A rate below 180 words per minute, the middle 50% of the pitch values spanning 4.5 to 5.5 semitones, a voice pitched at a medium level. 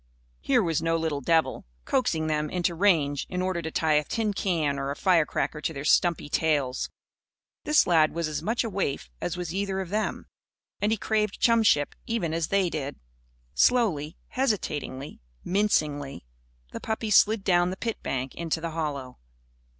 Yes: average, 170 wpm; average, 4.9 semitones; medium, 165 Hz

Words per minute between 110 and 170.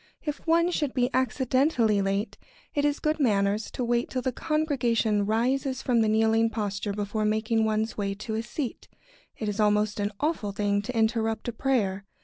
No: average, 180 wpm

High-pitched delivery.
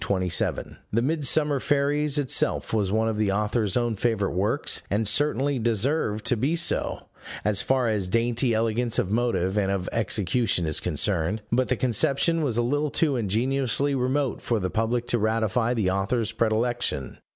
No: low, 115 Hz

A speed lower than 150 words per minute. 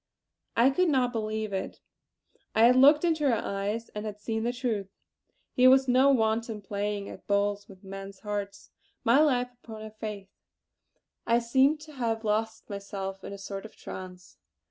No: average, 170 wpm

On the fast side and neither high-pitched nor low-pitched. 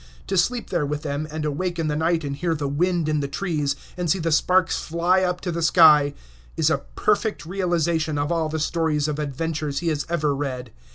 Yes: fast, 220 wpm; medium, 160 Hz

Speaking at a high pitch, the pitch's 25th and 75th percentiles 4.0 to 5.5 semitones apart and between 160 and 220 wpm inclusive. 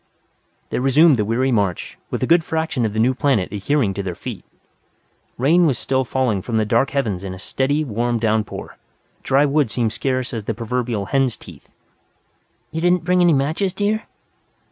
No: low, 130 Hz; average, 5.2 semitones; average, 185 wpm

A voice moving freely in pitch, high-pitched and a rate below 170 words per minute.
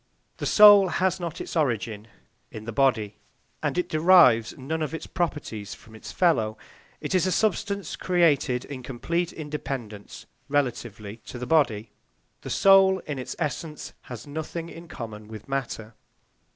No: wide, 7.1 semitones; medium, 145 Hz; average, 150 wpm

